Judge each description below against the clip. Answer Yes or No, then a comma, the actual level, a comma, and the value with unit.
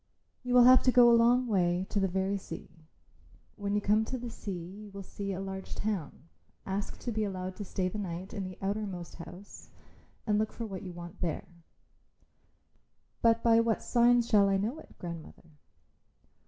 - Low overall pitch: No, high, 200 Hz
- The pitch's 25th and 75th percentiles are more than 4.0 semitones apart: No, average, 3.5 semitones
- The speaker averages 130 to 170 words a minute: No, average, 190 wpm